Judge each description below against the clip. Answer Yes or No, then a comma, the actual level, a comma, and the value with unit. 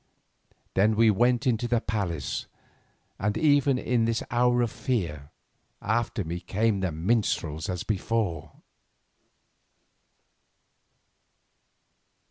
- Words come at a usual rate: No, slow, 100 wpm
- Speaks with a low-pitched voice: Yes, low, 110 Hz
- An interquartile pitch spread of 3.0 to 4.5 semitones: No, average, 5.0 semitones